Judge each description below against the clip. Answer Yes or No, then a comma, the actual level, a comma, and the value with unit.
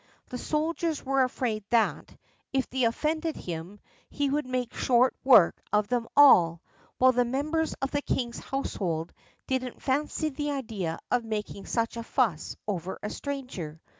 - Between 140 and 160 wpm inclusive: Yes, average, 155 wpm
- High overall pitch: Yes, very high, 250 Hz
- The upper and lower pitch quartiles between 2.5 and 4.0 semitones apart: No, average, 4.8 semitones